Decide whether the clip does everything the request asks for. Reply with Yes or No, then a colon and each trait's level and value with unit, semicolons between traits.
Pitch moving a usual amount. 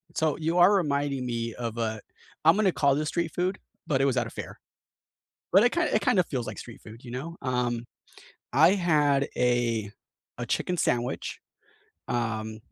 No: wide, 5.8 semitones